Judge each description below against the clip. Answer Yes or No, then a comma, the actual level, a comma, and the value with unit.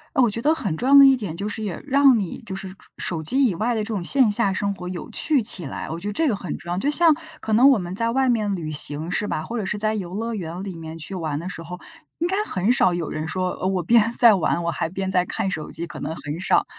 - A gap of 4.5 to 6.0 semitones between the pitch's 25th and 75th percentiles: Yes, average, 5.1 semitones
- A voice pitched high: Yes, high, 195 Hz